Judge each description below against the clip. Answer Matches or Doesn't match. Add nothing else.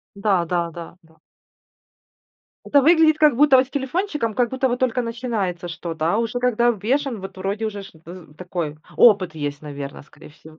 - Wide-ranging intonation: Matches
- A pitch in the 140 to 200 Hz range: Doesn't match